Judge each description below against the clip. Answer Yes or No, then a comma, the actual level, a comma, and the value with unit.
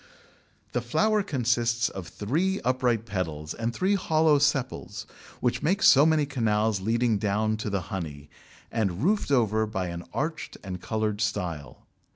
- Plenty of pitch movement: Yes, wide, 5.9 semitones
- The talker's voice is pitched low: Yes, low, 115 Hz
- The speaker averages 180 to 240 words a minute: No, average, 150 wpm